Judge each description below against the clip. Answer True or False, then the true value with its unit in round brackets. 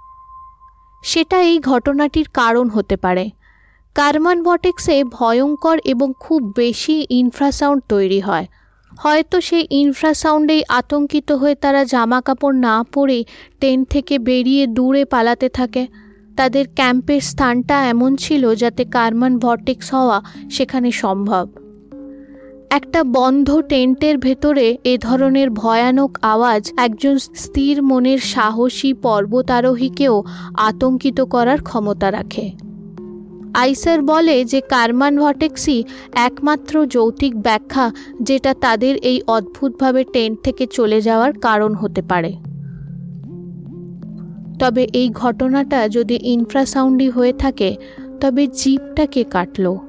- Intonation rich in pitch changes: False (3.4 semitones)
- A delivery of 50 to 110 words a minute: True (105 wpm)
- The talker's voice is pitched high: True (255 Hz)